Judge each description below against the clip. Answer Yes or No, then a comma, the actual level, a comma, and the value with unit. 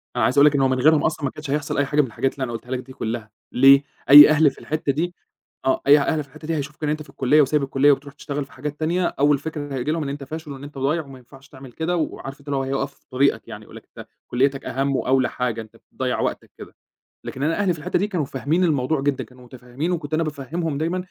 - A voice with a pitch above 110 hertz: Yes, medium, 140 Hz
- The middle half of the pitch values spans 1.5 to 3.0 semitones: Yes, narrow, 2.5 semitones